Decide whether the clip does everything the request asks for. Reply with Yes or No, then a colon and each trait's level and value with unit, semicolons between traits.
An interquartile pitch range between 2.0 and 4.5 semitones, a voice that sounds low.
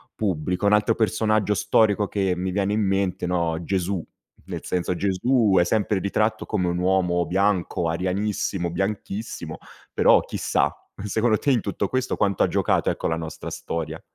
Yes: average, 2.9 semitones; very low, 95 Hz